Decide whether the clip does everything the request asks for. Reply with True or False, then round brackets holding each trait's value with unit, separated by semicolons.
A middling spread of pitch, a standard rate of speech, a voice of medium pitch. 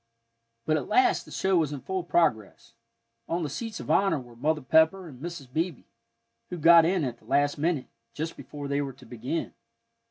True (3.9 semitones; 195 wpm; 155 Hz)